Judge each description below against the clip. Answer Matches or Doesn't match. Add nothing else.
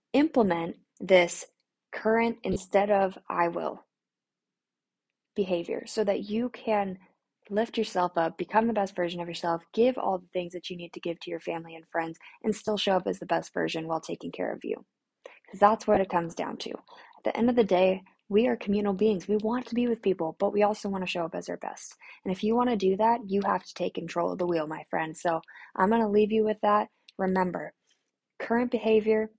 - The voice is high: Matches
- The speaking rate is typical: Doesn't match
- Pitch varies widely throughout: Doesn't match